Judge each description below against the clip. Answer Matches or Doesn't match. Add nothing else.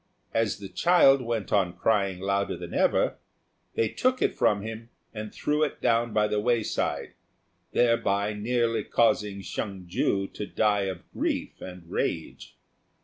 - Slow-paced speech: Doesn't match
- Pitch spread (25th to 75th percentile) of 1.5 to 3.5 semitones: Matches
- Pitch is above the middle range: Doesn't match